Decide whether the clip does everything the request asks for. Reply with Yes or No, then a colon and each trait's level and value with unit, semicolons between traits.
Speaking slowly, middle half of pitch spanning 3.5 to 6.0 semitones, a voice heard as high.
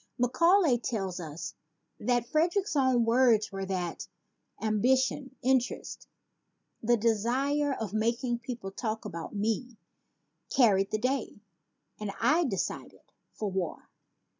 Yes: slow, 115 wpm; average, 4.0 semitones; high, 235 Hz